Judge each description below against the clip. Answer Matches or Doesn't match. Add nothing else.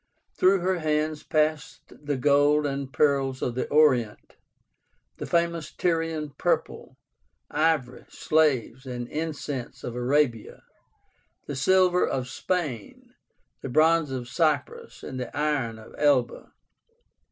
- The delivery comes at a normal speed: Doesn't match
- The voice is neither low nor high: Matches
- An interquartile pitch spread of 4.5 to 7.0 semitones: Doesn't match